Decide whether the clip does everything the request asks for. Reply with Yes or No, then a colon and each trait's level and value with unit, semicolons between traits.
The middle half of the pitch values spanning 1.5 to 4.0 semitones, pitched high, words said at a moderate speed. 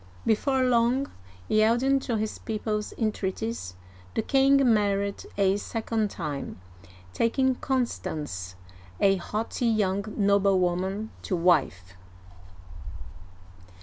No: average, 3.6 semitones; high, 210 Hz; slow, 90 wpm